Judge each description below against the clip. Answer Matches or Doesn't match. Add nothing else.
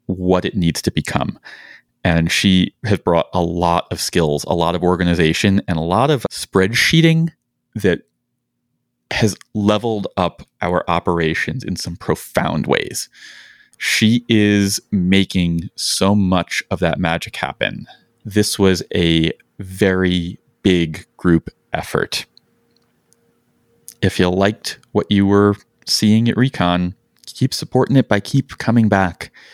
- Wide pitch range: Doesn't match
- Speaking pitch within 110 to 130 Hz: Doesn't match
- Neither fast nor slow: Doesn't match